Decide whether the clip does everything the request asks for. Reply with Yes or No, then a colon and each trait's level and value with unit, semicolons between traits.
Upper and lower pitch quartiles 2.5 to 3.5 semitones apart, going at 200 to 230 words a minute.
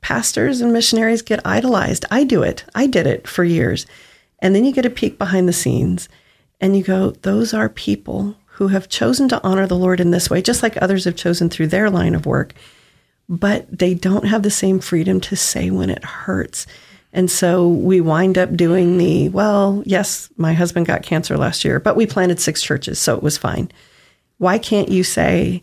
Yes: average, 3.1 semitones; fast, 205 wpm